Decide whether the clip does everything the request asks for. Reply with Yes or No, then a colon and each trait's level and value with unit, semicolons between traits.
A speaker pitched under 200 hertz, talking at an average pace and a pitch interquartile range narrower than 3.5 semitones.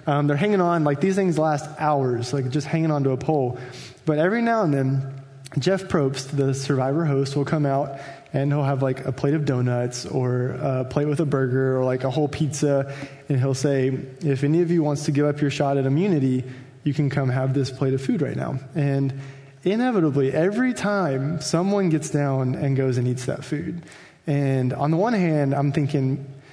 No: medium, 140 Hz; fast, 210 wpm; narrow, 2.5 semitones